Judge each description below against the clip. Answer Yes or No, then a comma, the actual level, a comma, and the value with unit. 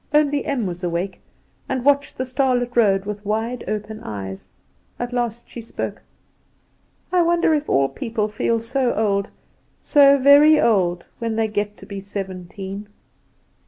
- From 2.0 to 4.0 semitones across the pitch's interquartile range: No, average, 4.7 semitones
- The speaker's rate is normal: Yes, average, 150 wpm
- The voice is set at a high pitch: Yes, high, 225 Hz